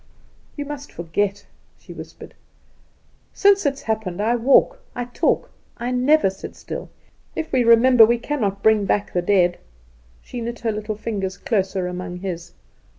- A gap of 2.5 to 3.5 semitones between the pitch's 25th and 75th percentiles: No, average, 4.4 semitones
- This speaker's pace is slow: No, average, 155 wpm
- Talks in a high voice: Yes, high, 220 Hz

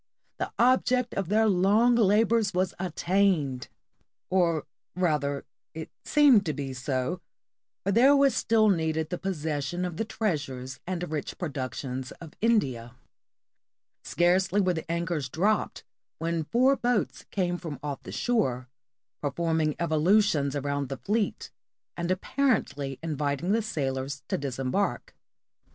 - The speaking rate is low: Yes, slow, 130 wpm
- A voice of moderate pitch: Yes, medium, 170 Hz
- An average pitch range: No, wide, 6.3 semitones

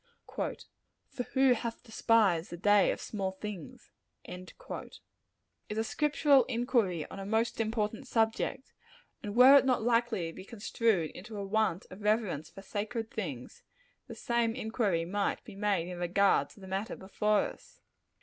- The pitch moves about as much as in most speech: Yes, average, 3.4 semitones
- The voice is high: Yes, high, 215 Hz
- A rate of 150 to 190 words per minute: Yes, average, 155 wpm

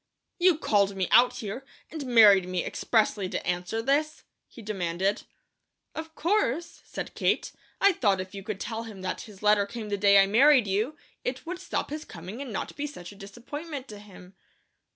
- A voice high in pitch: Yes, high, 215 Hz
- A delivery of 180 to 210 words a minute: Yes, average, 190 wpm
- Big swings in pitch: Yes, wide, 5.8 semitones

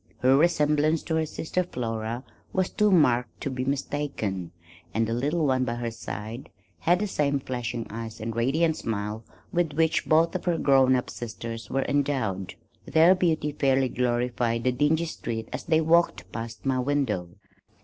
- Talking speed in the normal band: Yes, average, 170 wpm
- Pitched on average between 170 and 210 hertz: No, low, 130 Hz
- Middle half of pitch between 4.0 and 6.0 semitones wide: Yes, average, 5.2 semitones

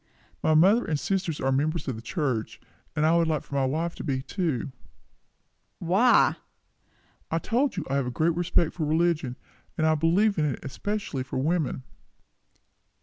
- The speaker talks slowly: No, average, 170 wpm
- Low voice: No, medium, 160 Hz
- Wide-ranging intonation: No, average, 4.0 semitones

